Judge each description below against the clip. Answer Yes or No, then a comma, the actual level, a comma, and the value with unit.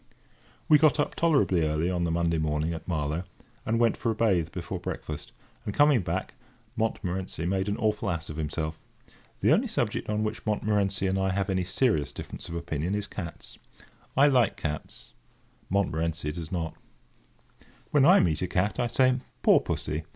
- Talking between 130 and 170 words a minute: No, average, 180 wpm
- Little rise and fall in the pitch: No, average, 4.6 semitones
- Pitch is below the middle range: Yes, very low, 95 Hz